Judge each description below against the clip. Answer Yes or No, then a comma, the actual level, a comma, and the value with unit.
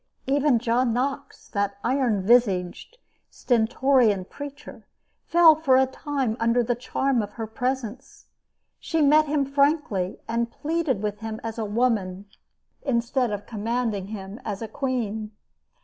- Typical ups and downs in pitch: Yes, average, 4.1 semitones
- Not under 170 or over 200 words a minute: No, slow, 135 wpm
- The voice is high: Yes, high, 235 Hz